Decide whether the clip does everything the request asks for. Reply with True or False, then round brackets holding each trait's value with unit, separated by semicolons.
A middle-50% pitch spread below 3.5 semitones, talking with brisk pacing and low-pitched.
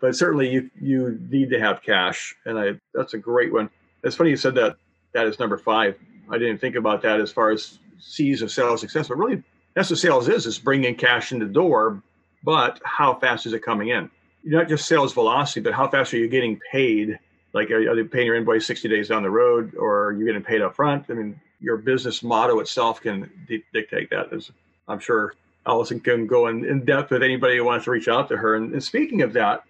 True (3.0 semitones; 240 wpm; 120 Hz)